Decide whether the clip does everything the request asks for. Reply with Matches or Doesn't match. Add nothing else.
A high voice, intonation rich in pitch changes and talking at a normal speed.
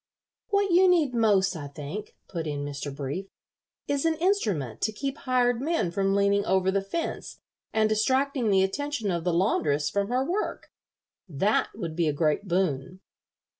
Matches